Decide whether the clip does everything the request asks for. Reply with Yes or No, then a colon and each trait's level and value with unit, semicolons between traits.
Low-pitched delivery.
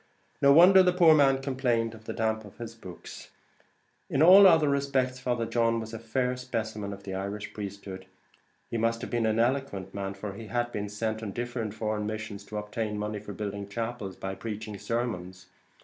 Yes: low, 110 Hz